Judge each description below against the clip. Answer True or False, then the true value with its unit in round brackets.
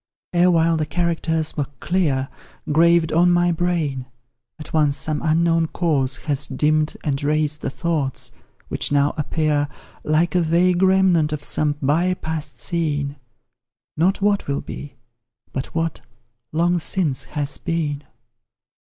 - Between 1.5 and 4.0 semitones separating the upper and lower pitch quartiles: True (2.7 semitones)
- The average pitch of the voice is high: False (155 Hz)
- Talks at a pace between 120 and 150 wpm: True (135 wpm)